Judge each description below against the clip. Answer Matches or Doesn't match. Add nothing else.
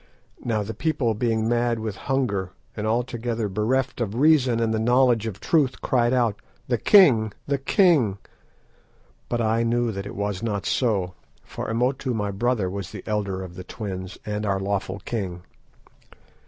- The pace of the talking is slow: Doesn't match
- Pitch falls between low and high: Doesn't match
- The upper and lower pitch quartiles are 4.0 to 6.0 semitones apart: Doesn't match